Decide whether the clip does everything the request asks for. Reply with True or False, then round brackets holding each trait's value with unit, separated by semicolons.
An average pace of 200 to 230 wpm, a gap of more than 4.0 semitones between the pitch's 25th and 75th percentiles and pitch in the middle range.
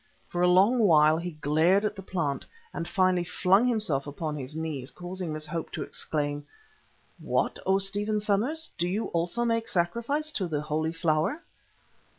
False (165 wpm; 5.0 semitones; 175 Hz)